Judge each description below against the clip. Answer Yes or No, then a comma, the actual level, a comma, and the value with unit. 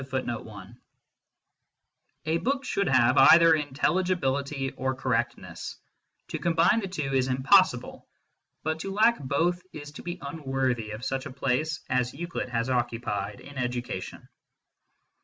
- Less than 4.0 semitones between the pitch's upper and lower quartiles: No, average, 4.7 semitones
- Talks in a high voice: No, low, 135 Hz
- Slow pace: Yes, slow, 130 wpm